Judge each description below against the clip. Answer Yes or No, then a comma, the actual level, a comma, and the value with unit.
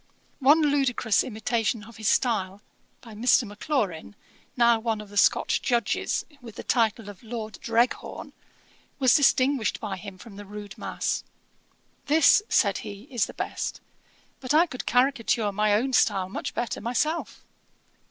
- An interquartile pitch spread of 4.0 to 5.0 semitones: No, average, 3.6 semitones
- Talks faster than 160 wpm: No, average, 150 wpm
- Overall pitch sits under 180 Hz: No, high, 230 Hz